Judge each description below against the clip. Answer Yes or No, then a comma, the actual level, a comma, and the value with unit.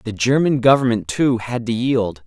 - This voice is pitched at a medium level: No, low, 120 Hz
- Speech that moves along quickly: No, average, 185 wpm